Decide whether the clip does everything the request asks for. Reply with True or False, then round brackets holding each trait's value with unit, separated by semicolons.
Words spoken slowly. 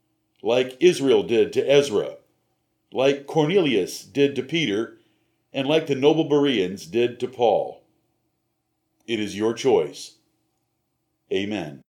True (115 wpm)